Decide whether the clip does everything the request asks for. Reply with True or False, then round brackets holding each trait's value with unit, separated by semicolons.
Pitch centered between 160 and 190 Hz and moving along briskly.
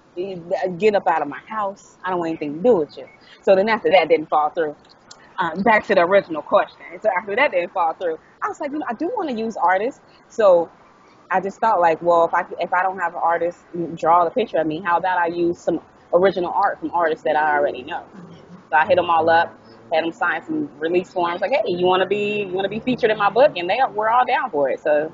True (185 Hz; 265 wpm)